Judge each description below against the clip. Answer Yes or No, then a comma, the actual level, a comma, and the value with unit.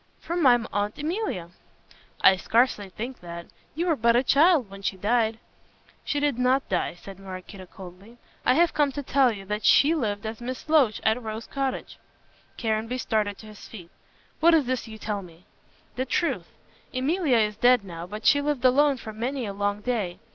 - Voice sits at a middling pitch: No, high, 230 Hz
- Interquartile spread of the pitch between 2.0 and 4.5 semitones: No, average, 5.0 semitones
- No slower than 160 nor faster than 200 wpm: Yes, average, 190 wpm